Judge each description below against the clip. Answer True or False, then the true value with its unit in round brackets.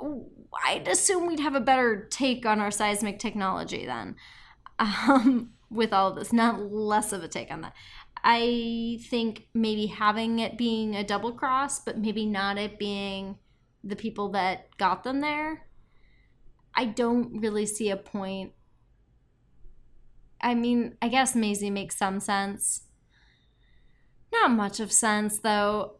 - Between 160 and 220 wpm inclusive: False (150 wpm)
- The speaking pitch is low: False (215 Hz)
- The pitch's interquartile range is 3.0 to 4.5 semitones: False (2.6 semitones)